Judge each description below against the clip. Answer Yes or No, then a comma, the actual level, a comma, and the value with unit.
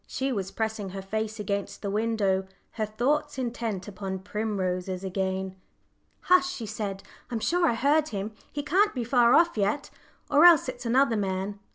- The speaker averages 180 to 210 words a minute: No, average, 170 wpm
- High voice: Yes, high, 220 Hz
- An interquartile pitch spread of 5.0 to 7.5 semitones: Yes, average, 5.3 semitones